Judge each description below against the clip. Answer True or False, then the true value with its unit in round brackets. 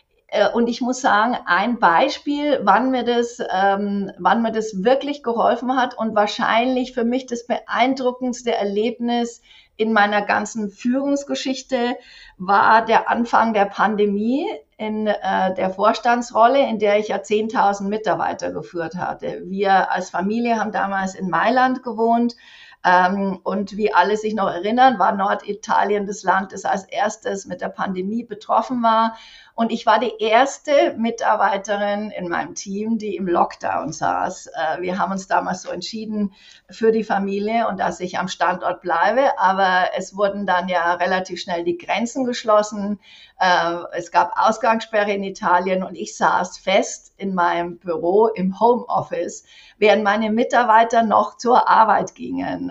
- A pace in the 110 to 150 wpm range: True (145 wpm)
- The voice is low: False (210 Hz)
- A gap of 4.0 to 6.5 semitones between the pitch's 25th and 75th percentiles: False (3.6 semitones)